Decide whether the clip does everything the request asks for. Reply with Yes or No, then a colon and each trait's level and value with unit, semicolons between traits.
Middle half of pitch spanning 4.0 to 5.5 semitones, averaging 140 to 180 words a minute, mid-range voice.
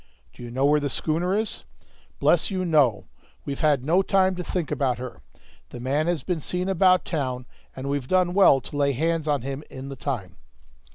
No: average, 5.1 semitones; fast, 205 wpm; medium, 150 Hz